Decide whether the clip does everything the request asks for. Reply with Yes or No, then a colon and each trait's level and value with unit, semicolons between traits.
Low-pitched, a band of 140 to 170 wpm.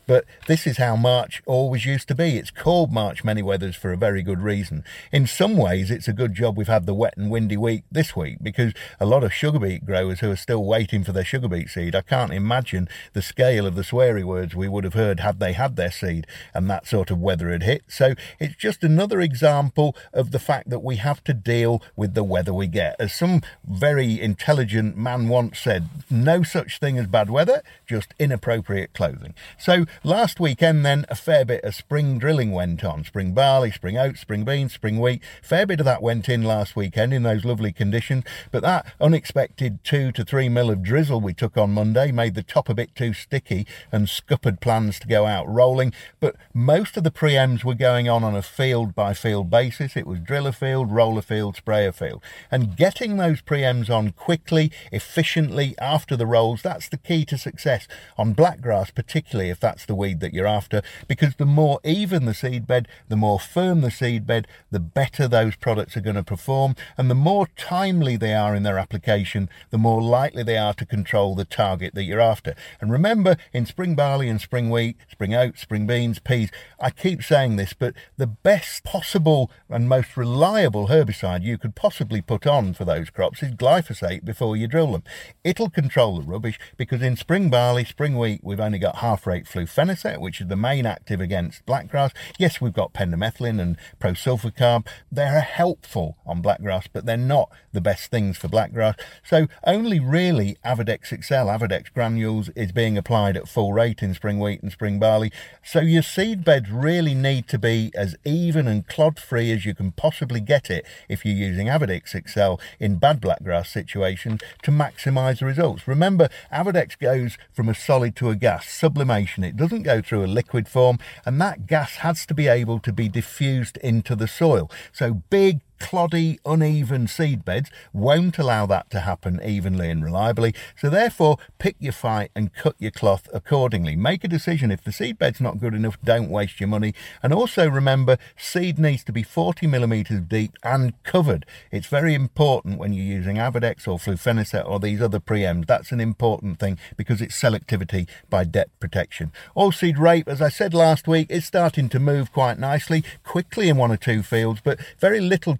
No: low, 120 Hz; average, 200 wpm